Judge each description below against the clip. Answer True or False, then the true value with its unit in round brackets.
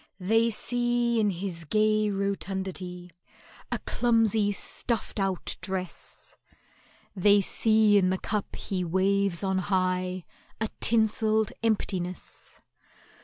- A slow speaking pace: True (105 wpm)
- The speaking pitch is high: True (200 Hz)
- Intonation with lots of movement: False (2.8 semitones)